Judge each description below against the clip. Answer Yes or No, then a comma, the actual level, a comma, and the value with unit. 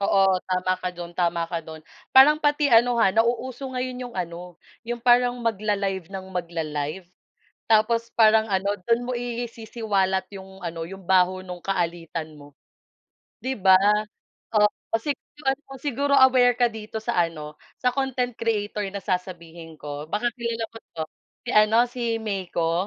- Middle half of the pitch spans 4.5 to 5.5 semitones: Yes, average, 5.2 semitones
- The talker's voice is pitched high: Yes, high, 205 Hz